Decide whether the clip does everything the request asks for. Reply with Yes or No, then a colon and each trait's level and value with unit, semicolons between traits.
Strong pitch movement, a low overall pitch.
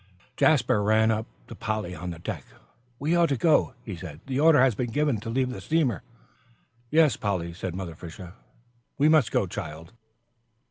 Yes: wide, 7.6 semitones; low, 110 Hz